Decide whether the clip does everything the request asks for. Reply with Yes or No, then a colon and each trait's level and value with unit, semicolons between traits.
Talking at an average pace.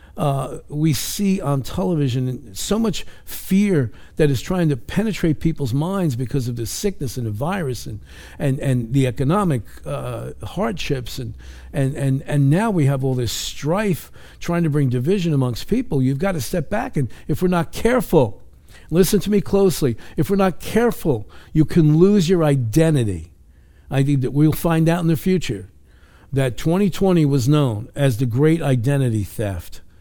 Yes: average, 170 wpm